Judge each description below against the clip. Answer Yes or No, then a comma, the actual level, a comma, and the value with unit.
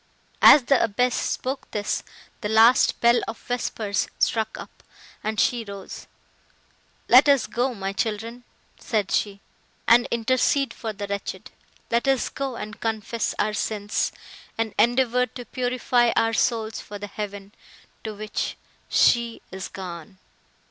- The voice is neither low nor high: No, high, 225 Hz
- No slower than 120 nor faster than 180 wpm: Yes, average, 140 wpm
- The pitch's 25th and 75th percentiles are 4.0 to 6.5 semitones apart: No, average, 2.8 semitones